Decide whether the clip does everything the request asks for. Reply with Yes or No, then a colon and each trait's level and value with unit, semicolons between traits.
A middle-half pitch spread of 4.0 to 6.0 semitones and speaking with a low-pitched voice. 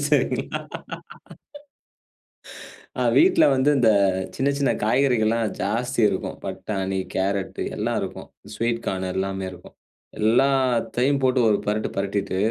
Yes: average, 4.9 semitones; low, 110 Hz